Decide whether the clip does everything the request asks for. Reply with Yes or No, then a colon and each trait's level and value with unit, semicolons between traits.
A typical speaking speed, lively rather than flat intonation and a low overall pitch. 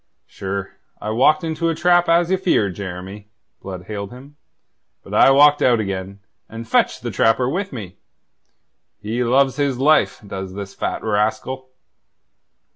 Yes: average, 150 wpm; wide, 6.6 semitones; low, 115 Hz